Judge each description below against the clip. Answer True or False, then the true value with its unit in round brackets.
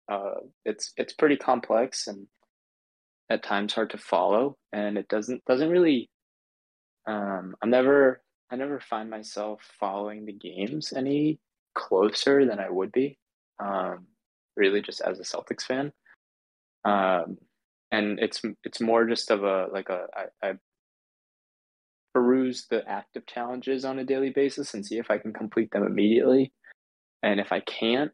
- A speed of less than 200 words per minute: True (150 wpm)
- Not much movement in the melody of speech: False (4.3 semitones)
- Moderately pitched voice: False (115 Hz)